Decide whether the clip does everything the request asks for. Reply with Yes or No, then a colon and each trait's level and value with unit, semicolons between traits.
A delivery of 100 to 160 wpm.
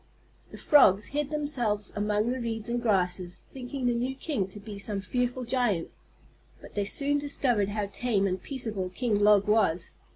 No: average, 170 wpm